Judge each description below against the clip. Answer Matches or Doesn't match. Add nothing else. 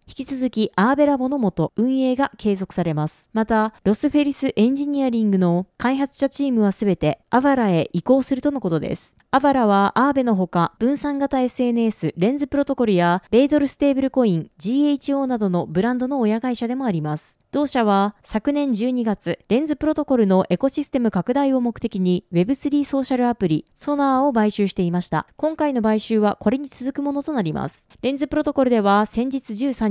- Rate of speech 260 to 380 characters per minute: Doesn't match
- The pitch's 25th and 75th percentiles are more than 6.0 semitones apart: Doesn't match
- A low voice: Doesn't match